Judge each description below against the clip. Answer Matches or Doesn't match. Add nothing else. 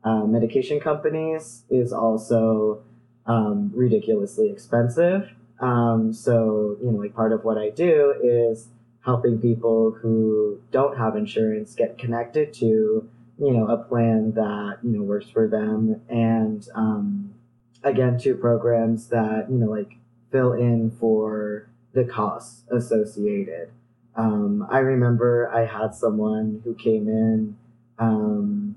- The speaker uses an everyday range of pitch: Doesn't match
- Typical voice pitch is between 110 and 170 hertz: Matches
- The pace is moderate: Doesn't match